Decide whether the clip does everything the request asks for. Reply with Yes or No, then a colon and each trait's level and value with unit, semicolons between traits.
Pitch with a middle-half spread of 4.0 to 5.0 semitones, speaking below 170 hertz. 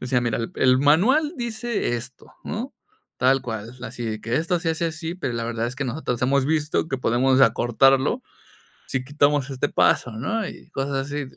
Yes: average, 4.7 semitones; low, 135 Hz